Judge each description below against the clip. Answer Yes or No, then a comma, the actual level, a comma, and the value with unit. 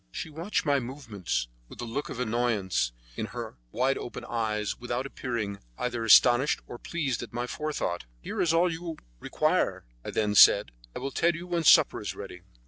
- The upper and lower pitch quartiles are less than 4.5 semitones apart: No, average, 5.0 semitones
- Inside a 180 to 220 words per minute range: Yes, average, 190 wpm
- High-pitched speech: No, low, 125 Hz